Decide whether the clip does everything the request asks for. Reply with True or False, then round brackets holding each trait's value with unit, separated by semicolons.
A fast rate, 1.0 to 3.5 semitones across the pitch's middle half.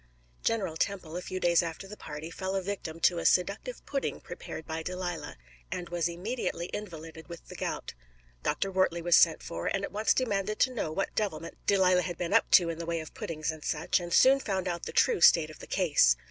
True (220 wpm; 3.1 semitones)